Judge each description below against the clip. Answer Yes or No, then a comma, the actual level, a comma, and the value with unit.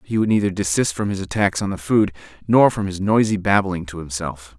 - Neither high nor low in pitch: No, very low, 95 Hz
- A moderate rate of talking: No, fast, 225 wpm